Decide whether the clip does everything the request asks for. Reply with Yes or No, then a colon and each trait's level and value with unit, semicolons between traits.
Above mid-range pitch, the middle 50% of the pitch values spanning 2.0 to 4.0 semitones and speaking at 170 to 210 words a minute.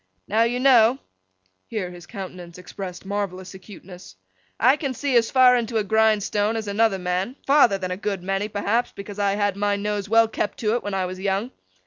Yes: high, 205 Hz; average, 2.9 semitones; average, 195 wpm